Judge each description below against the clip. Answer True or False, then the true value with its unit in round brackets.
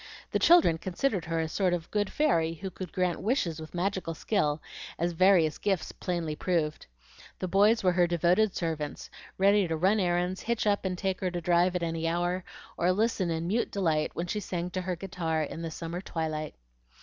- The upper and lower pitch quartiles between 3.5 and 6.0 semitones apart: False (2.6 semitones)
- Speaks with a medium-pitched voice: True (175 Hz)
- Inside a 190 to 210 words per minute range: True (195 wpm)